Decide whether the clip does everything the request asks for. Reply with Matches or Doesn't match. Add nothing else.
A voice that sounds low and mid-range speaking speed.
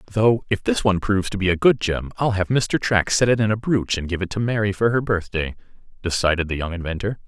Doesn't match